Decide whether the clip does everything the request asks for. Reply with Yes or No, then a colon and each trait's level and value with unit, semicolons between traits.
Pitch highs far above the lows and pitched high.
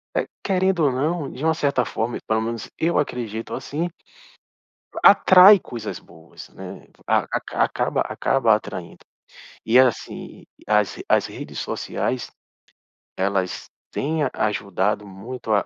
No: wide, 6.4 semitones; low, 120 Hz